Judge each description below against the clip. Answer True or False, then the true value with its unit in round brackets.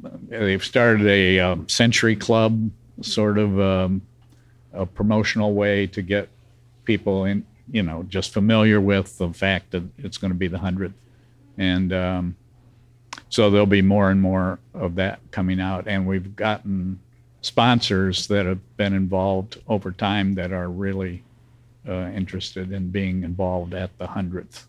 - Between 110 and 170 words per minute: True (155 wpm)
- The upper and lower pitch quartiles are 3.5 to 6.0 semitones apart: False (3.1 semitones)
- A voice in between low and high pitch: False (100 Hz)